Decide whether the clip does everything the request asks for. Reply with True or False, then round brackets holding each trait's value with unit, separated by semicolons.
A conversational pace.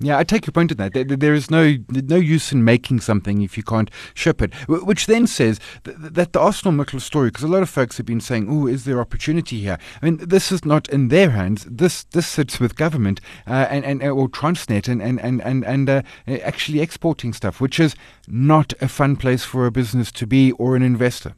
False (225 wpm)